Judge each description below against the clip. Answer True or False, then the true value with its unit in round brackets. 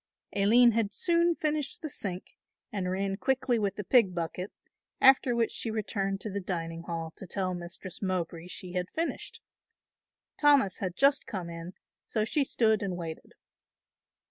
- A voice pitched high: True (195 Hz)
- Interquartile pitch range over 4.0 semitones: True (5.0 semitones)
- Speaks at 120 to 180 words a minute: True (160 wpm)